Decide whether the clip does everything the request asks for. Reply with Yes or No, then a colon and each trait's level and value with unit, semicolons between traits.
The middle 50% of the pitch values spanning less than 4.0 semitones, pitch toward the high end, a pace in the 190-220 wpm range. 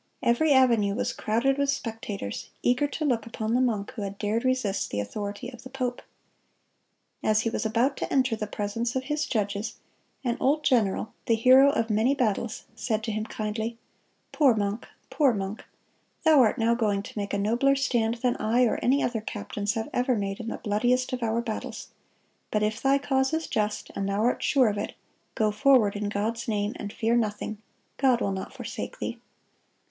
Yes: average, 3.4 semitones; high, 230 Hz; average, 195 wpm